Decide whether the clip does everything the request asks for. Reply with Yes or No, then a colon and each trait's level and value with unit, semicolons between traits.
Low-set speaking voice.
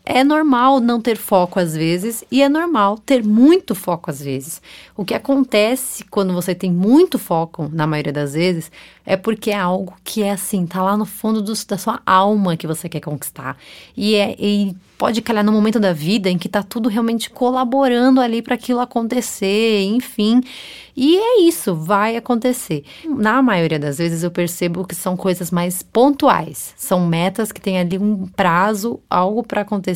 No: high, 205 Hz